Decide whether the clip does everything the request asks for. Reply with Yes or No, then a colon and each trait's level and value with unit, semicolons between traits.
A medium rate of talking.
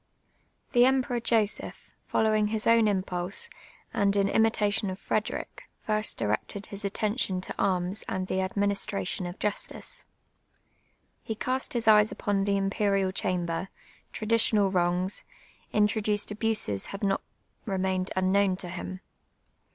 No: slow, 130 wpm